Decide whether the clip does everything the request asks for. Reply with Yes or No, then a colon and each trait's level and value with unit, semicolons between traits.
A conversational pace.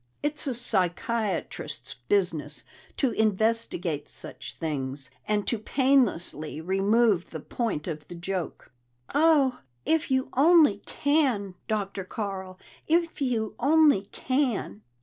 No: slow, 110 wpm